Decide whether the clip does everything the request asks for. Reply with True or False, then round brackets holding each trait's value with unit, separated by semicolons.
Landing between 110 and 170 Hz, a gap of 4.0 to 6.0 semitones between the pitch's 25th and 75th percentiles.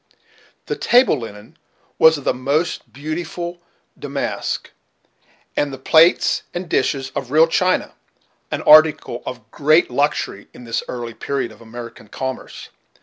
True (140 Hz; 4.8 semitones)